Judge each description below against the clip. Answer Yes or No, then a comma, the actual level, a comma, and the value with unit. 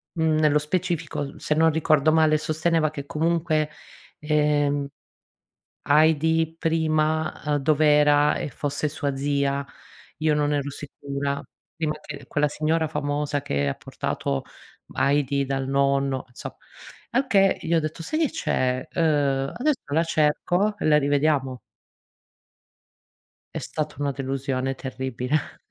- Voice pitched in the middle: Yes, medium, 150 Hz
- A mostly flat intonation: Yes, narrow, 2.2 semitones